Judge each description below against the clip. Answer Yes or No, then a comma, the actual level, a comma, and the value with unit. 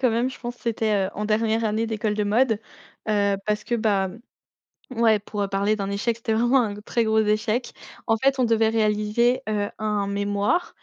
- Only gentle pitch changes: Yes, narrow, 1.9 semitones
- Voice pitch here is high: Yes, high, 215 Hz